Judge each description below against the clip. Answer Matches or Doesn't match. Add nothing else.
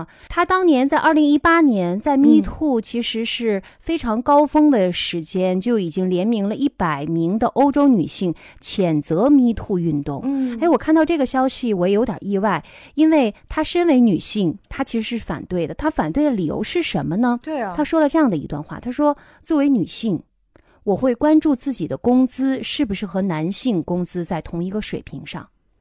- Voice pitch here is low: Doesn't match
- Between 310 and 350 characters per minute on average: Doesn't match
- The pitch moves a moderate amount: Doesn't match